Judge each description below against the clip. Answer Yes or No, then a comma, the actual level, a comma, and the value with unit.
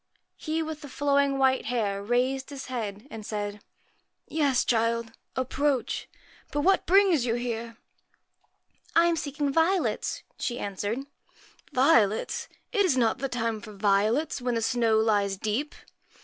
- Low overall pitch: No, high, 245 Hz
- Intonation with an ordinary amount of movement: Yes, average, 4.5 semitones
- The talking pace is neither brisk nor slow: Yes, average, 150 wpm